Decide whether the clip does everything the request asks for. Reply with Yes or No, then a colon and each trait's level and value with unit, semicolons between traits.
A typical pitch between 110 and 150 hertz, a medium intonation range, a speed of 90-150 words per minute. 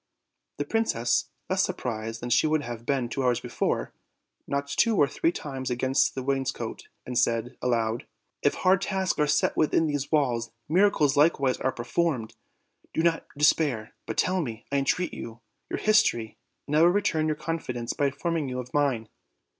No: medium, 140 Hz; average, 4.7 semitones; average, 180 wpm